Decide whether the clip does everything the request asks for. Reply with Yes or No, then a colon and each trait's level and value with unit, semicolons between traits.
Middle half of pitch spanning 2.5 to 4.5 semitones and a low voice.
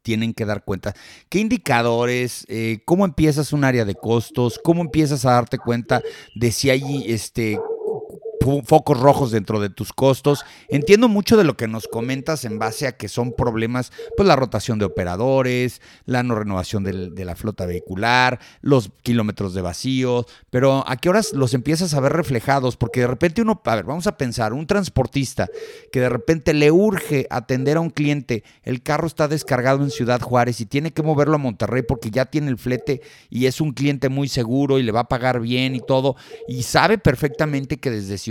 Yes: average, 4.1 semitones; low, 130 Hz